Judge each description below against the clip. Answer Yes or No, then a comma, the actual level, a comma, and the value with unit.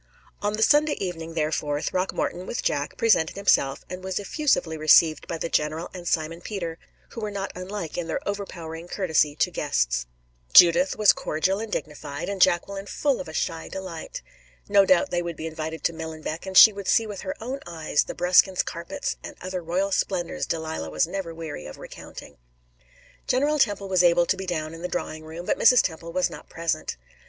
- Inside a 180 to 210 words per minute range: Yes, average, 195 wpm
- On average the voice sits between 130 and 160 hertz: No, medium, 175 Hz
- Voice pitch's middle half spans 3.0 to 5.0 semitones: Yes, average, 3.6 semitones